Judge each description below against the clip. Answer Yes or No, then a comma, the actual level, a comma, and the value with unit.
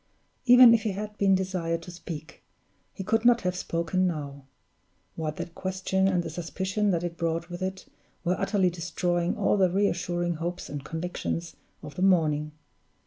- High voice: No, medium, 180 Hz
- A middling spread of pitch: No, narrow, 2.3 semitones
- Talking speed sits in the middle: Yes, average, 175 wpm